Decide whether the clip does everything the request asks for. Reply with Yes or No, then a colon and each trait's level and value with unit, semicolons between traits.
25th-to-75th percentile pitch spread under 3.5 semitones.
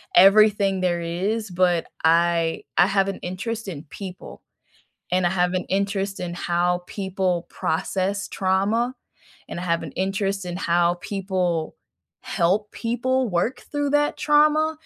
Yes: average, 3.0 semitones